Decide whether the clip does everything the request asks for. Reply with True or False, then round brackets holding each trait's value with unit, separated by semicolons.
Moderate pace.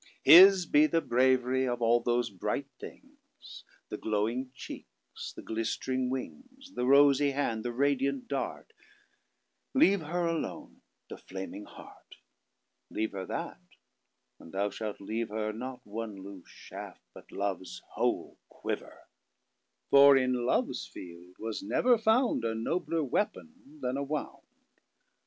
False (115 wpm)